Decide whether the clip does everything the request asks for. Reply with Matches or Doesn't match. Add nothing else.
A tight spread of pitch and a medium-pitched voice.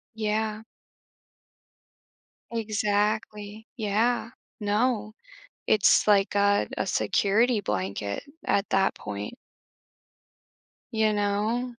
Doesn't match